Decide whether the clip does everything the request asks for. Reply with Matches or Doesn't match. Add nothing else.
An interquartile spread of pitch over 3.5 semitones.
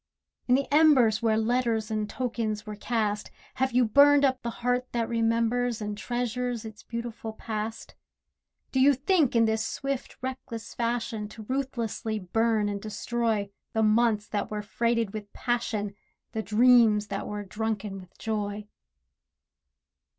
Doesn't match